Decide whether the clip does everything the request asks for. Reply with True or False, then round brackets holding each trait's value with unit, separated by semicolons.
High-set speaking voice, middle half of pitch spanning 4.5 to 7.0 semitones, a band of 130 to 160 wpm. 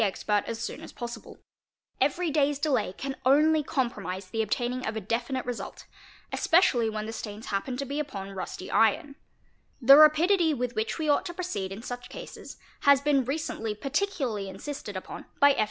False (250 Hz; 5.1 semitones; 180 wpm)